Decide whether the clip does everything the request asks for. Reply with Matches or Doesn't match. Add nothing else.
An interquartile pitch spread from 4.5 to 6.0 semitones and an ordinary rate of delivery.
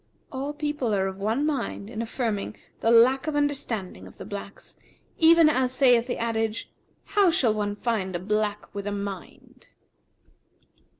Matches